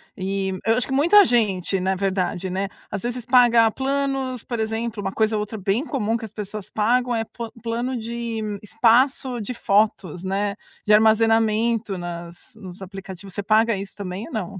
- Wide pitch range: No, average, 3.3 semitones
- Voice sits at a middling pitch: No, high, 220 Hz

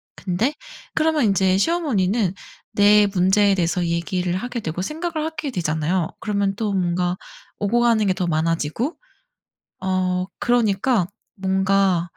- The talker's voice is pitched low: No, high, 195 Hz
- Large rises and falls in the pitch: No, average, 4.2 semitones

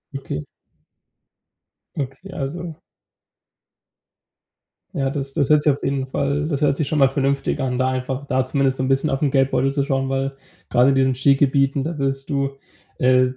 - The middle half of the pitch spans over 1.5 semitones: No, narrow, 1.0 semitones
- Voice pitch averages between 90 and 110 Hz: No, low, 135 Hz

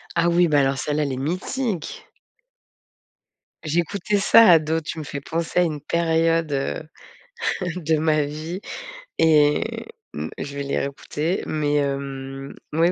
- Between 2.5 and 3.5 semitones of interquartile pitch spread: Yes, average, 2.9 semitones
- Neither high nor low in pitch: Yes, medium, 155 Hz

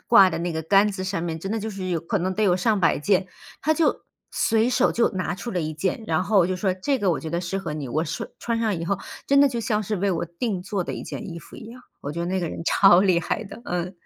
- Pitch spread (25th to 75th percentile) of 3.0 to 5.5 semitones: Yes, average, 3.7 semitones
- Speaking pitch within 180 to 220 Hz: Yes, high, 190 Hz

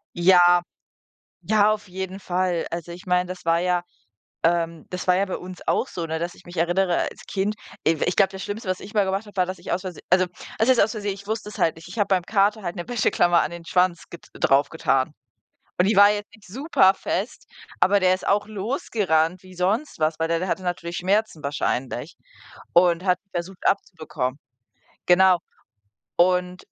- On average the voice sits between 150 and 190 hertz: Yes, medium, 185 Hz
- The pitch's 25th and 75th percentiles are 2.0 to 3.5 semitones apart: Yes, narrow, 2.6 semitones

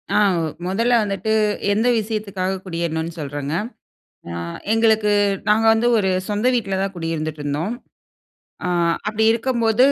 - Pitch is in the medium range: No, high, 200 Hz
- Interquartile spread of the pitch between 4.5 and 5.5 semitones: Yes, average, 4.8 semitones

